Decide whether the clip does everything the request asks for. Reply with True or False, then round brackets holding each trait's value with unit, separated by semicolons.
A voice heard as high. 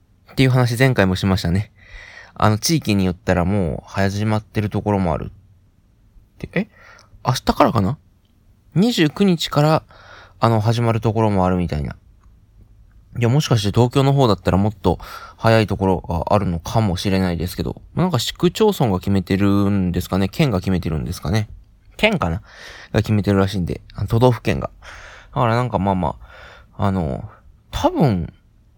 False (100 Hz)